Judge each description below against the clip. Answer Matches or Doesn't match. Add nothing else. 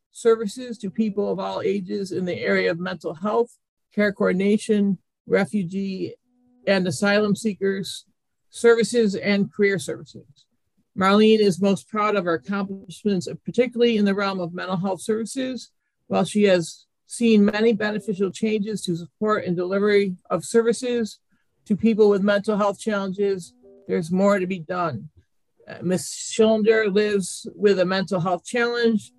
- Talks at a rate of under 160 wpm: Matches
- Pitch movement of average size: Doesn't match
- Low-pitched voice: Doesn't match